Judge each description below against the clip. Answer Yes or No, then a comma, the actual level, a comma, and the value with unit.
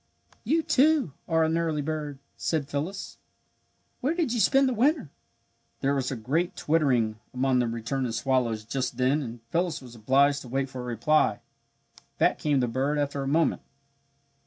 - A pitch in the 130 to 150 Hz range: Yes, medium, 140 Hz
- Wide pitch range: No, average, 4.3 semitones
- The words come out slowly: No, average, 170 wpm